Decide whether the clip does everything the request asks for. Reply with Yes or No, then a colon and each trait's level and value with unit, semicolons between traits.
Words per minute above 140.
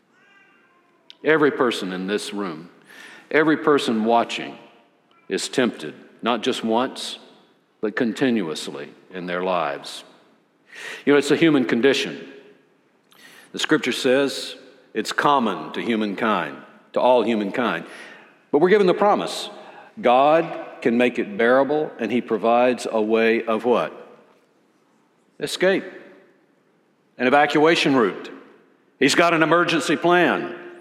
No: slow, 115 wpm